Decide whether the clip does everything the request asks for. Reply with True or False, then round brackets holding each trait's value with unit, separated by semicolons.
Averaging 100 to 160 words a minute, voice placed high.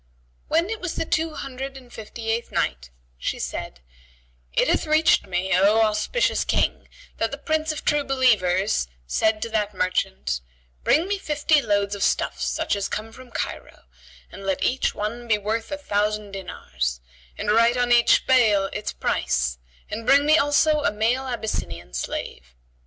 False (170 wpm; 225 Hz)